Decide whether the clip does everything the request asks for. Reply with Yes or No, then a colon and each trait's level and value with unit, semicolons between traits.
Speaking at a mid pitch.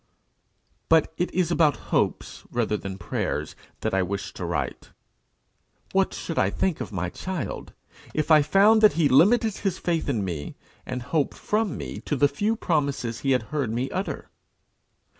Yes: medium, 145 Hz